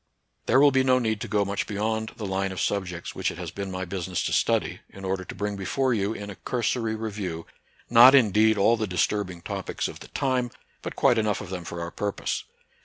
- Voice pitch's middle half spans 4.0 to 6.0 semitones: No, average, 3.0 semitones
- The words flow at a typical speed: No, fast, 230 wpm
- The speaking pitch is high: No, low, 105 Hz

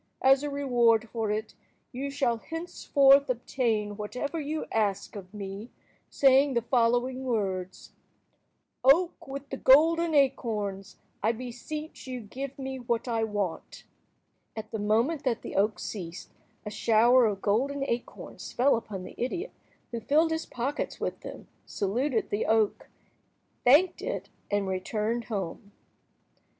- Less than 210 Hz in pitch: No, high, 240 Hz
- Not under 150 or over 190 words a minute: No, average, 140 wpm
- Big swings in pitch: No, average, 4.6 semitones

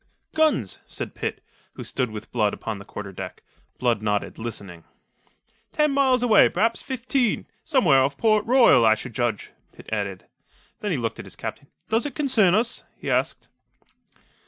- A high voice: No, medium, 140 Hz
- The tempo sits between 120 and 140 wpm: No, average, 165 wpm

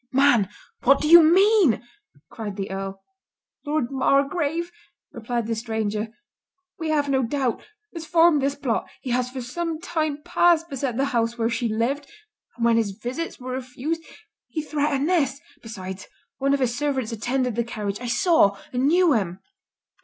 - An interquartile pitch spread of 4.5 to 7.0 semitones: Yes, average, 4.9 semitones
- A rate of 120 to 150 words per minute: No, average, 160 wpm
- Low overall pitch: No, very high, 260 Hz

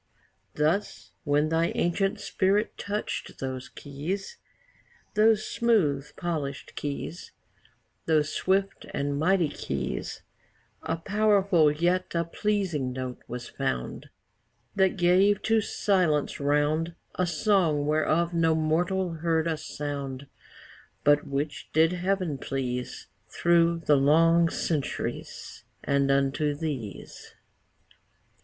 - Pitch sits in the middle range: Yes, medium, 160 Hz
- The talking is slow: Yes, slow, 105 wpm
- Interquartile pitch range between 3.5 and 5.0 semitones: Yes, average, 4.2 semitones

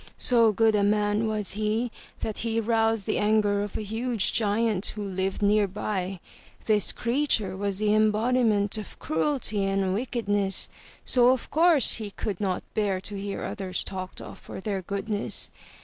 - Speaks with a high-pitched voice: Yes, high, 210 Hz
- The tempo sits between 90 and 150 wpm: No, average, 160 wpm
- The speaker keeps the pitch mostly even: Yes, narrow, 2.1 semitones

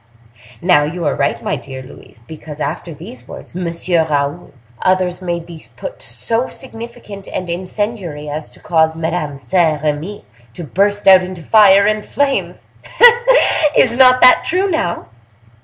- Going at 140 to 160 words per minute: Yes, average, 155 wpm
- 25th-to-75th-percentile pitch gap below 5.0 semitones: No, wide, 5.4 semitones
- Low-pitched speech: No, medium, 180 Hz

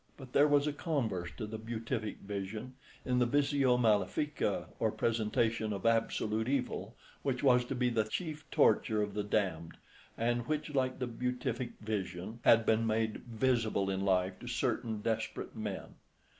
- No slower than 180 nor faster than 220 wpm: No, average, 160 wpm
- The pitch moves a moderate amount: Yes, average, 3.1 semitones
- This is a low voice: Yes, low, 115 Hz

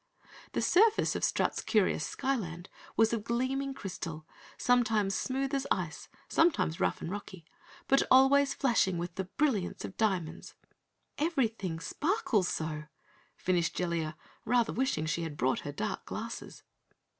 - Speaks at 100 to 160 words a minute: Yes, slow, 135 wpm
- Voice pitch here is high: Yes, high, 210 Hz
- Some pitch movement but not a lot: No, wide, 7.8 semitones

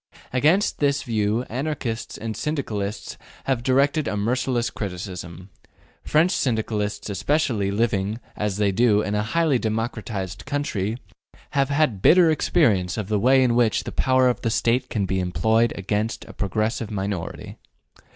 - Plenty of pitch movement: No, average, 4.2 semitones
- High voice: No, low, 110 Hz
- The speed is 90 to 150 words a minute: Yes, average, 145 wpm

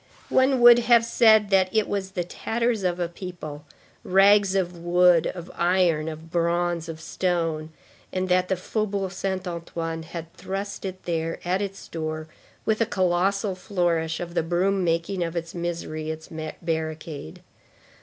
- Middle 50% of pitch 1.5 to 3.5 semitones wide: Yes, average, 2.9 semitones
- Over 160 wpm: No, average, 155 wpm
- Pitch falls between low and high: Yes, medium, 175 Hz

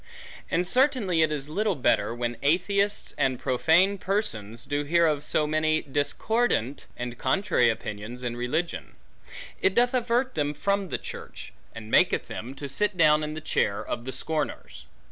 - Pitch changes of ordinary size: No, wide, 7.7 semitones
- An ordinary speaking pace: Yes, average, 165 wpm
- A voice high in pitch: No, medium, 155 Hz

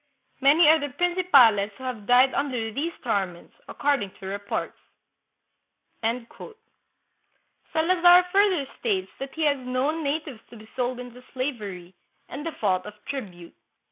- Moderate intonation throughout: No, wide, 6.2 semitones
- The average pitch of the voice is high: Yes, very high, 255 Hz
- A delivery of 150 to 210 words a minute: No, slow, 135 wpm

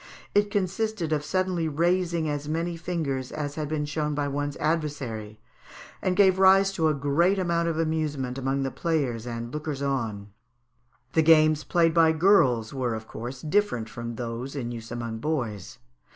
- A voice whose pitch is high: No, medium, 150 Hz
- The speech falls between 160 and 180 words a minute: Yes, average, 165 wpm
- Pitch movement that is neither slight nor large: Yes, average, 4.9 semitones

